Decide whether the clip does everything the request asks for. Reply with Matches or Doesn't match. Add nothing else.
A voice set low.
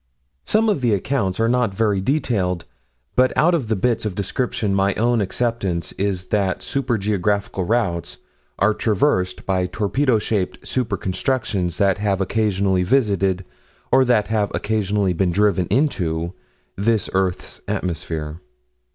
Matches